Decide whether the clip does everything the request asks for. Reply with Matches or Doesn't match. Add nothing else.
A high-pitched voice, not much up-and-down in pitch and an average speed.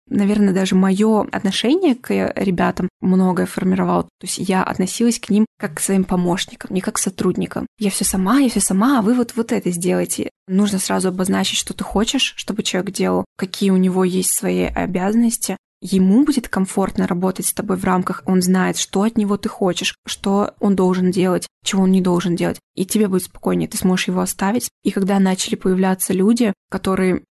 Doesn't match